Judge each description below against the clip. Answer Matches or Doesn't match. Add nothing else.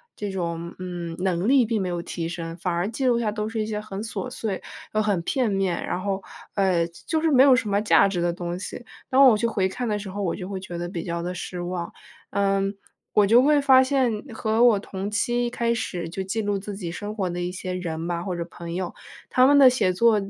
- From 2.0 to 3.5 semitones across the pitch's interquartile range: Doesn't match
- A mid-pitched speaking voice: Doesn't match